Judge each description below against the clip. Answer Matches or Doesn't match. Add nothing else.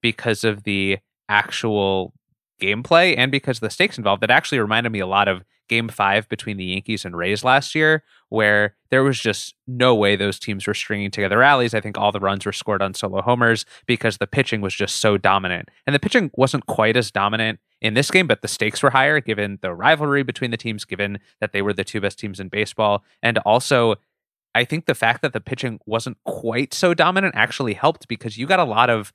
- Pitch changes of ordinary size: Matches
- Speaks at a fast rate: Matches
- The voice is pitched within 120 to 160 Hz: Doesn't match